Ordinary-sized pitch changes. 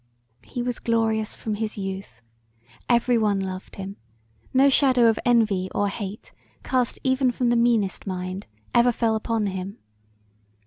Yes: average, 3.5 semitones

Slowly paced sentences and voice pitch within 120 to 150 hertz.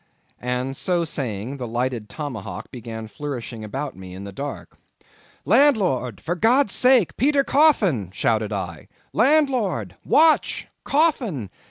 Yes: slow, 125 wpm; low, 135 Hz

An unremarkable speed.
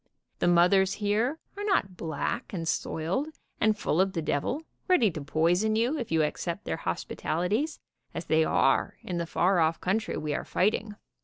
Yes: average, 175 wpm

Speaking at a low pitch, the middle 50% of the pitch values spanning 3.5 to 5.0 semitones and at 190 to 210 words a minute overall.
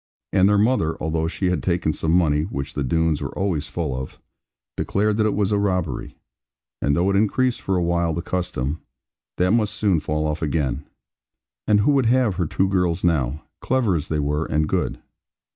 Yes: very low, 85 Hz; average, 4.5 semitones; average, 195 wpm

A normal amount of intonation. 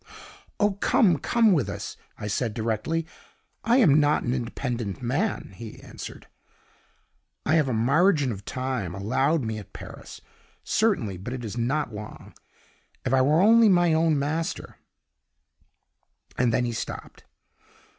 No: wide, 6.2 semitones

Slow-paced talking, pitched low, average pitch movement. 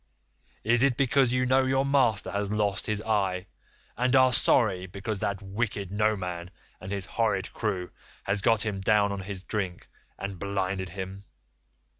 No: average, 160 wpm; low, 100 Hz; average, 3.0 semitones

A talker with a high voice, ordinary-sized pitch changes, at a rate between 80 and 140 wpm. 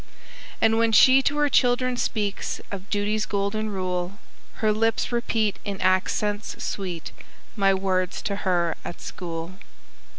Yes: high, 205 Hz; average, 3.1 semitones; slow, 135 wpm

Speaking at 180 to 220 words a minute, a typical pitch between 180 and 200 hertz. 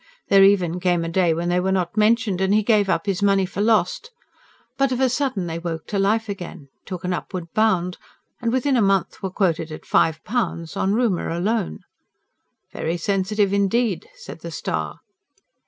Yes: average, 190 wpm; high, 190 Hz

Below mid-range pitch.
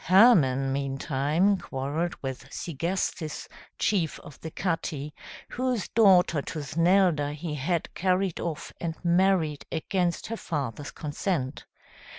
No: medium, 165 Hz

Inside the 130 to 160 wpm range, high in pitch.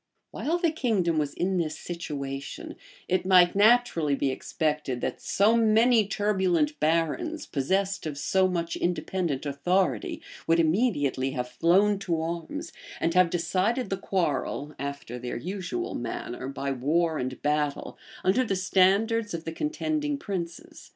No: average, 140 wpm; medium, 175 Hz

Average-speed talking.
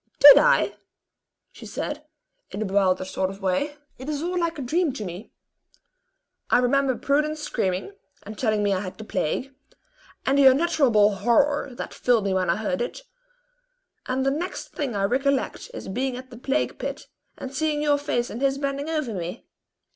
Yes: average, 185 wpm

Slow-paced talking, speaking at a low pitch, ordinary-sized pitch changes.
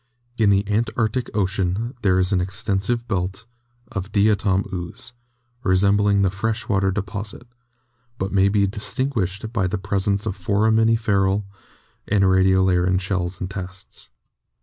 No: slow, 125 wpm; low, 100 Hz; narrow, 2.2 semitones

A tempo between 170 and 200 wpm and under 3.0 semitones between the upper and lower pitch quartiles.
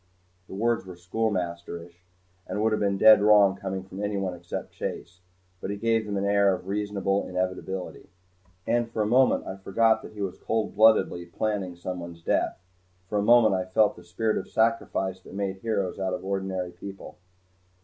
Yes: average, 180 wpm; narrow, 2.6 semitones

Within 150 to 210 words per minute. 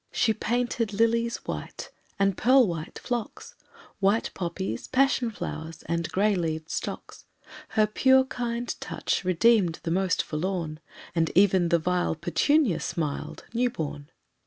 No: slow, 135 wpm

